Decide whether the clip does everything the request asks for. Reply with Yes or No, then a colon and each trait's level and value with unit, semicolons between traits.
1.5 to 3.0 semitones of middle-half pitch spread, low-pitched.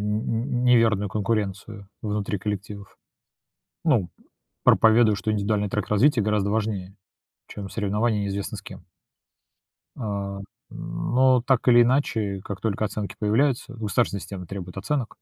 Yes: narrow, 2.5 semitones; low, 105 Hz